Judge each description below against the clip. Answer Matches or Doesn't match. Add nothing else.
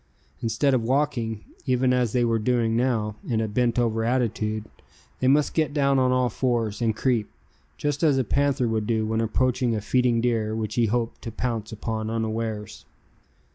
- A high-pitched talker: Doesn't match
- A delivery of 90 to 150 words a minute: Doesn't match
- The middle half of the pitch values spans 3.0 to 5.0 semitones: Doesn't match